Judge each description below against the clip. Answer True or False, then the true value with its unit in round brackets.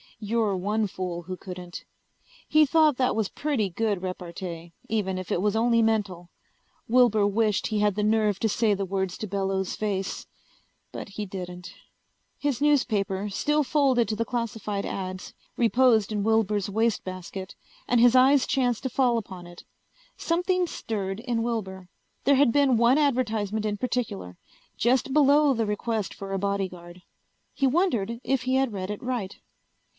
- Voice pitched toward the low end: False (215 Hz)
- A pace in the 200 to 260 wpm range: False (160 wpm)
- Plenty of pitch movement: False (4.3 semitones)